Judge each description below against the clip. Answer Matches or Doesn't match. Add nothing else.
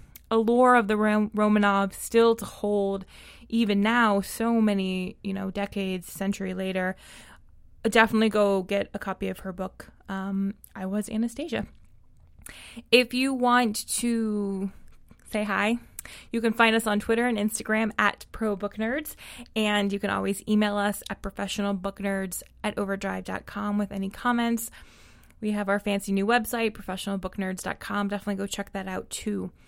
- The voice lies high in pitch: Matches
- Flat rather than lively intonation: Matches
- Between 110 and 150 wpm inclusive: Matches